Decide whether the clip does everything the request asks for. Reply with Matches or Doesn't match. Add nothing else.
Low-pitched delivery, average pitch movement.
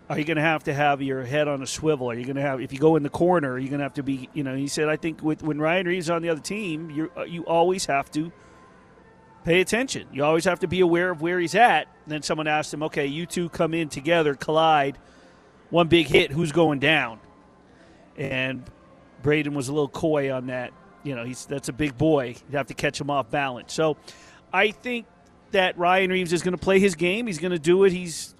Doesn't match